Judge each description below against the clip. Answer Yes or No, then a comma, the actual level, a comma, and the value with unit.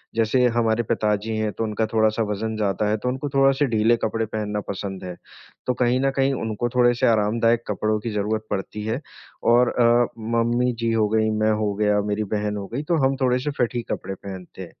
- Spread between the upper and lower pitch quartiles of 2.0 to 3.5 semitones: Yes, narrow, 2.4 semitones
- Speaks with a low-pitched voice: Yes, low, 110 Hz